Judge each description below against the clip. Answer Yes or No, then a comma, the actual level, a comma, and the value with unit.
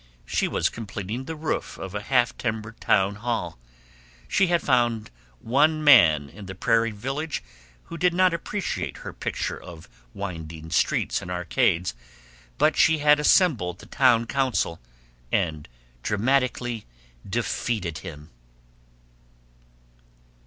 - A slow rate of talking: Yes, slow, 125 wpm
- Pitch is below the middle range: Yes, low, 115 Hz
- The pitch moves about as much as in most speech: No, wide, 7.2 semitones